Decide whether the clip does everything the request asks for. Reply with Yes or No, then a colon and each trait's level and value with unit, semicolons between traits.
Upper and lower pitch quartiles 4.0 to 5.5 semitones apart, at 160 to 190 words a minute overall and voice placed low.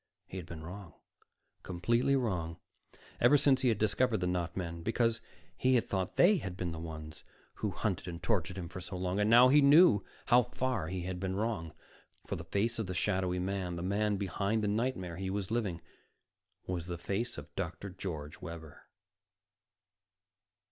Yes: average, 4.3 semitones; average, 185 wpm; very low, 95 Hz